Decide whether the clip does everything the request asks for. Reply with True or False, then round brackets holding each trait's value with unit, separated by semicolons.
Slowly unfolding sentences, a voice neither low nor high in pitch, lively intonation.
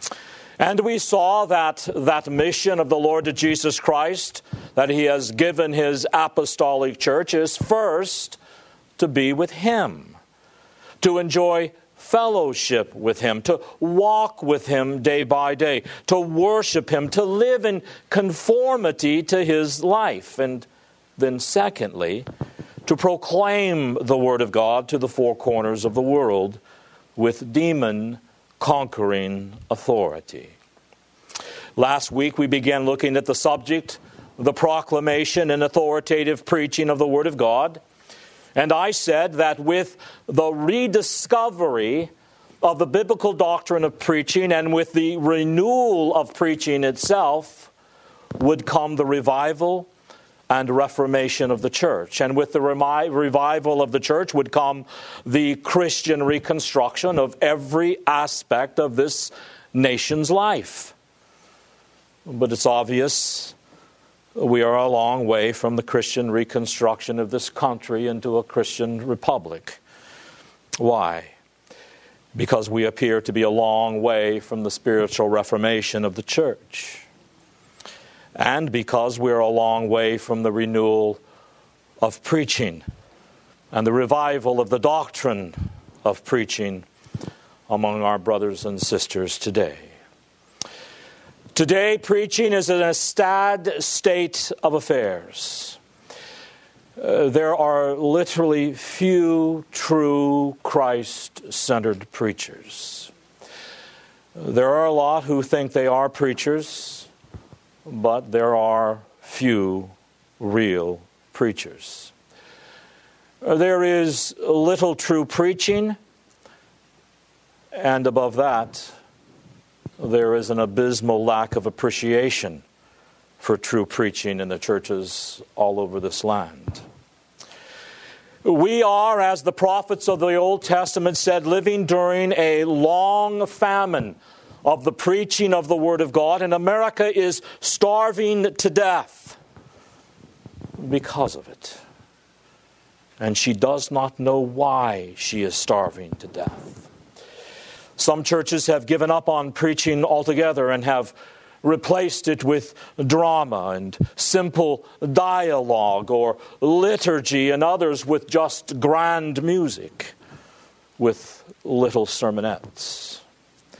True (120 wpm; 150 Hz; 5.9 semitones)